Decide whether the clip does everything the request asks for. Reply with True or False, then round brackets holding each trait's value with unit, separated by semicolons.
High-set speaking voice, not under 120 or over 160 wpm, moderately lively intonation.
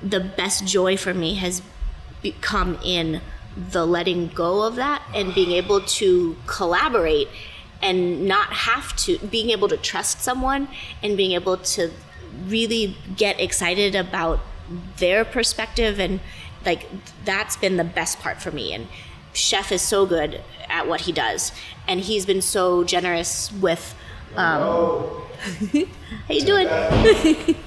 True (195 Hz; 140 wpm; 4.3 semitones)